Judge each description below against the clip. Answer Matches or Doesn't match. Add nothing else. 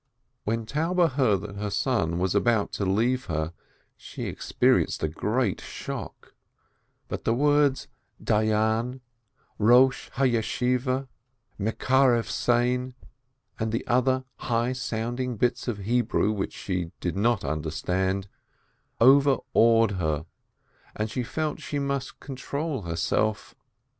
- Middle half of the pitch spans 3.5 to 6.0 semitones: Matches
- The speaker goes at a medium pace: Doesn't match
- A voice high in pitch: Doesn't match